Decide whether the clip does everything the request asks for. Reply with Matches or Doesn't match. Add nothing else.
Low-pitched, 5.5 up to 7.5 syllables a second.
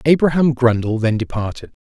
Matches